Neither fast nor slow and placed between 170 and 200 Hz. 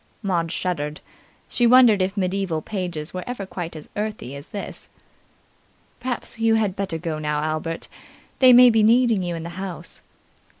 Yes: average, 165 wpm; medium, 185 Hz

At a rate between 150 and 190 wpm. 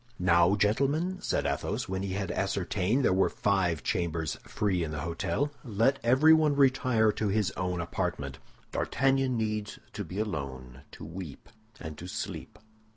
Yes: average, 155 wpm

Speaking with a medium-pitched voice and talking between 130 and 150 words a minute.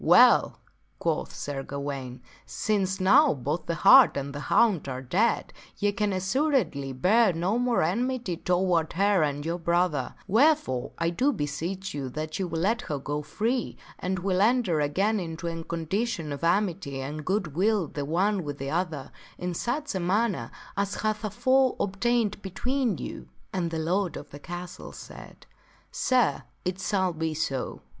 No: medium, 180 Hz; average, 170 wpm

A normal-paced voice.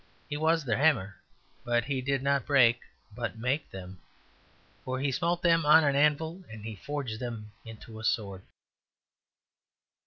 Yes: average, 155 wpm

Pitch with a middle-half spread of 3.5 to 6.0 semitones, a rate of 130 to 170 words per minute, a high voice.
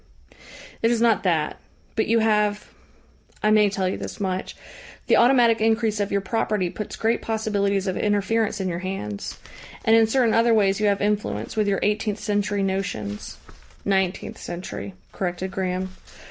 No: average, 2.7 semitones; average, 160 wpm; high, 205 Hz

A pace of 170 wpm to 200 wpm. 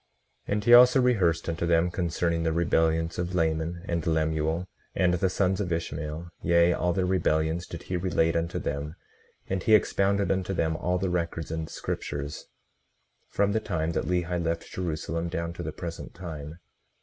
Yes: average, 175 wpm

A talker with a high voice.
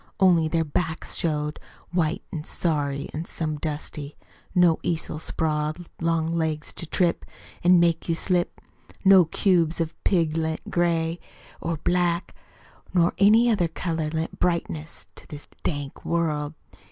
No: medium, 165 Hz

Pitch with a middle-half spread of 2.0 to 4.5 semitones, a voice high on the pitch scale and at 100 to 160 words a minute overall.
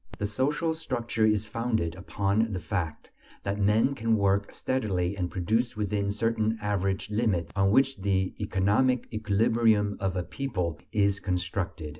No: average, 2.8 semitones; low, 105 Hz; average, 145 wpm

